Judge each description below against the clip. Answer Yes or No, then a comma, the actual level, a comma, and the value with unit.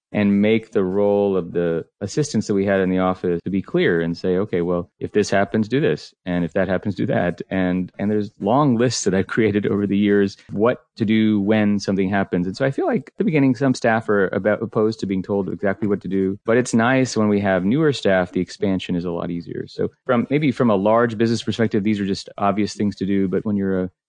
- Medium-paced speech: No, fast, 250 wpm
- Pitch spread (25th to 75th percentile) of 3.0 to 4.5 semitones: No, narrow, 2.6 semitones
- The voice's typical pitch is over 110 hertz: No, low, 100 Hz